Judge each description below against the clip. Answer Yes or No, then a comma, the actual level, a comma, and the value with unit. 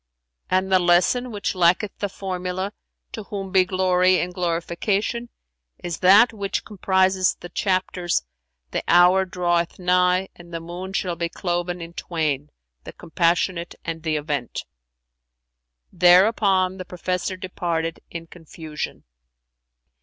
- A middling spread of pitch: No, narrow, 2.0 semitones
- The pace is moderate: No, slow, 130 wpm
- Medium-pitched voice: Yes, medium, 180 Hz